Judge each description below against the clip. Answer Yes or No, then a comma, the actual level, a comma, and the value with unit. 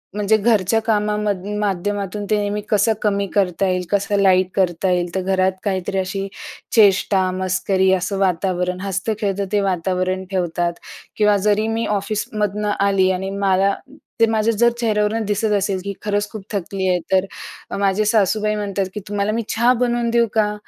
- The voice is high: Yes, high, 200 Hz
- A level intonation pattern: Yes, narrow, 1.9 semitones